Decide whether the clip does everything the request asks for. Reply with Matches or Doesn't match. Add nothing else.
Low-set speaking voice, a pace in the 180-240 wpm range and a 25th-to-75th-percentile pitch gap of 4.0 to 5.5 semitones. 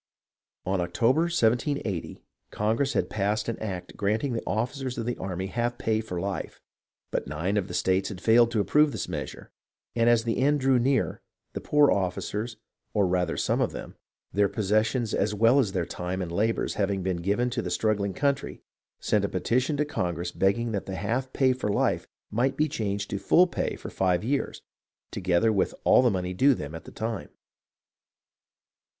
Matches